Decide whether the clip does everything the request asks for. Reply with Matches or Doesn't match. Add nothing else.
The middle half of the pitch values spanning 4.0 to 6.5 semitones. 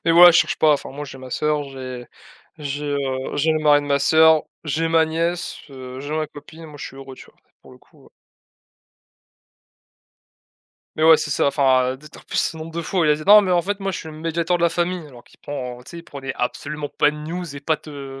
Doesn't match